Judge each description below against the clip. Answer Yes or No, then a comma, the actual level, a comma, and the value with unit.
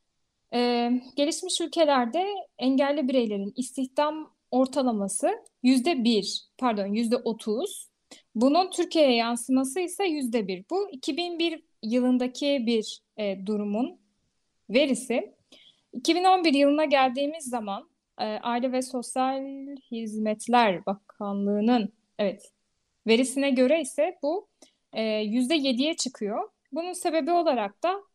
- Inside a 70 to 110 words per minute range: Yes, average, 100 wpm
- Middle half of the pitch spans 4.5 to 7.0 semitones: Yes, wide, 5.4 semitones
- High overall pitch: Yes, very high, 260 Hz